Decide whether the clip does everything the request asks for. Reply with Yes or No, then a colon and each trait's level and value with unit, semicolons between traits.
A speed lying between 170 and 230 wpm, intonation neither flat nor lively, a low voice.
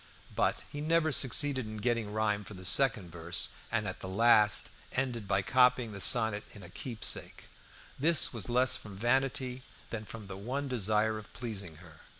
Yes: average, 175 wpm; average, 3.9 semitones; low, 110 Hz